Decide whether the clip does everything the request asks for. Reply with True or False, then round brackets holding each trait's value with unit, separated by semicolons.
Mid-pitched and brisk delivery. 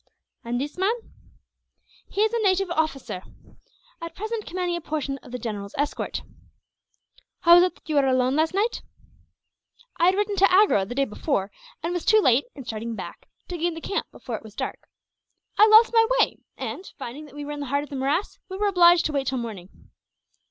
False (310 Hz; 210 wpm)